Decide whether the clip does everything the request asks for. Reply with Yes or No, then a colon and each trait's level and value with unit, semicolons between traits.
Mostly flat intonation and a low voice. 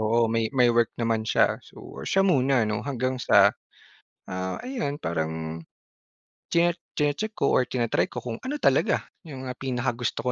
No: average, 3.8 semitones; low, 120 Hz